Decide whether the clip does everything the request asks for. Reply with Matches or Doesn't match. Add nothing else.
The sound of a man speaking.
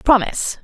Doesn't match